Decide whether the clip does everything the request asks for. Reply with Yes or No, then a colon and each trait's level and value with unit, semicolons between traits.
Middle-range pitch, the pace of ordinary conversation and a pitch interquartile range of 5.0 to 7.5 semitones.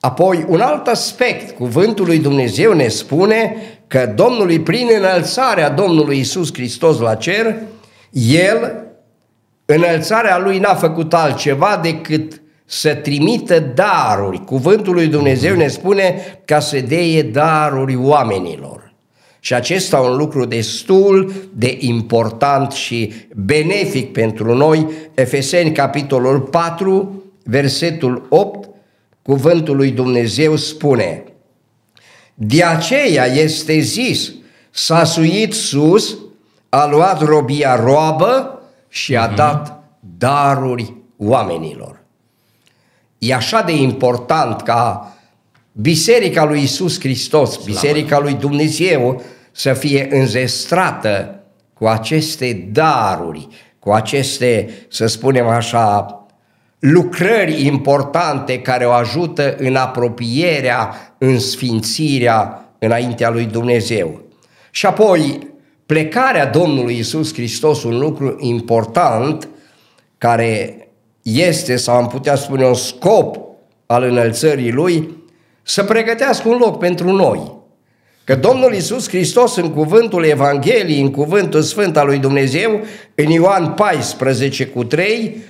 No: medium, 145 Hz; slow, 105 wpm; average, 5.3 semitones